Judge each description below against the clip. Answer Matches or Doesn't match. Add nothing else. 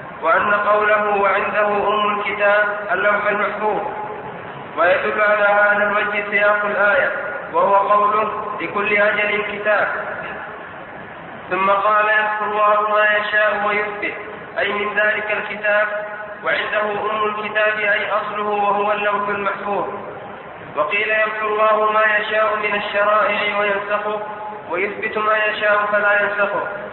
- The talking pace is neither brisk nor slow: Matches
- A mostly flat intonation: Matches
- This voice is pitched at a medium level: Doesn't match